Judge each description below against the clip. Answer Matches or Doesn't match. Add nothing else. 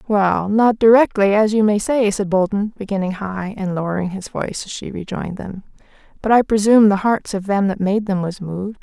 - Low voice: Doesn't match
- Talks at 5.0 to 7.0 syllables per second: Matches